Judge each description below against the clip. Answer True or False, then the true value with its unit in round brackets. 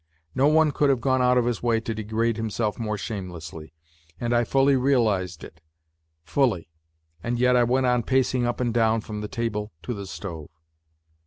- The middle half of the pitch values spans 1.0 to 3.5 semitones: True (3.1 semitones)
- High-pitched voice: False (115 Hz)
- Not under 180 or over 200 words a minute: True (185 wpm)